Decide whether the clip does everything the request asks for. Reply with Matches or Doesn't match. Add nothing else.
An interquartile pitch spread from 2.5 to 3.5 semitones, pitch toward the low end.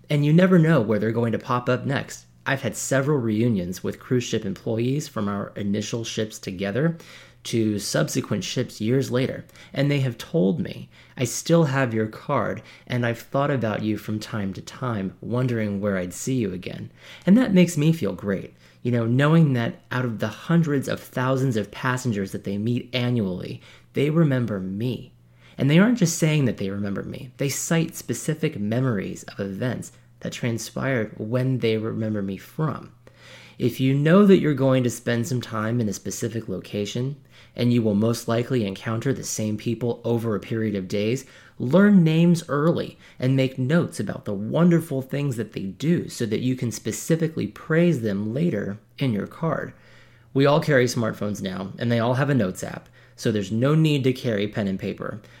Doesn't match